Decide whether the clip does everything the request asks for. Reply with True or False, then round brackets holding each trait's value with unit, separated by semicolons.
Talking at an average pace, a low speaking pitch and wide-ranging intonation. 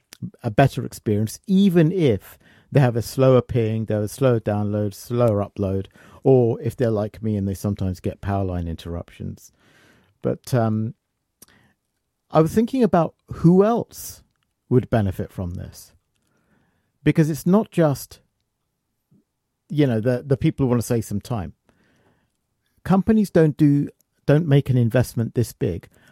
True (150 wpm; 120 Hz; 5.7 semitones)